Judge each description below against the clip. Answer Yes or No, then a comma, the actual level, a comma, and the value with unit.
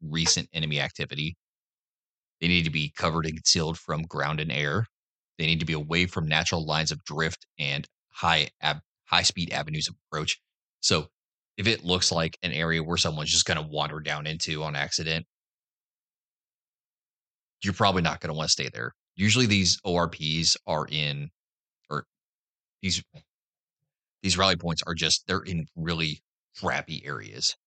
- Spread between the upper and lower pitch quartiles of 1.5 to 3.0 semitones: Yes, narrow, 2.4 semitones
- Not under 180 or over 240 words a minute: No, average, 160 wpm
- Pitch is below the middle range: Yes, very low, 80 Hz